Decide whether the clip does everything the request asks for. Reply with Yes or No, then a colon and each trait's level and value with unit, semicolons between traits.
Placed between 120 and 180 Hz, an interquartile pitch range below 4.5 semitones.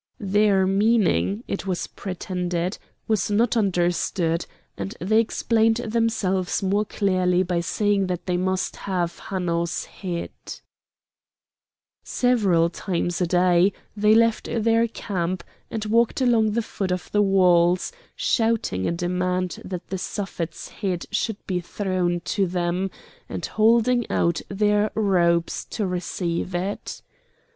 No: high, 190 Hz; average, 3.2 semitones